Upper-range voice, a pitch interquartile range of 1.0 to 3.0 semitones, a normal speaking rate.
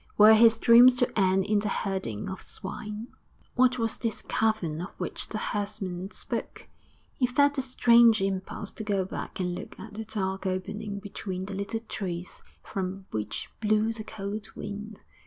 Yes: high, 210 Hz; average, 2.7 semitones; average, 170 wpm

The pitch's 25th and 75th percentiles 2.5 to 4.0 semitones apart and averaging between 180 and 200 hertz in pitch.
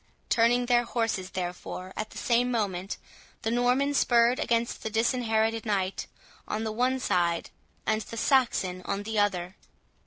No: average, 3.6 semitones; high, 225 Hz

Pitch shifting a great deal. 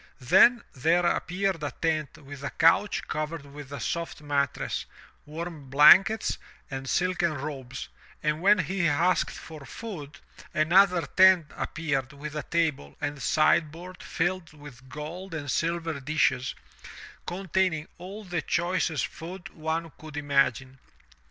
No: average, 3.6 semitones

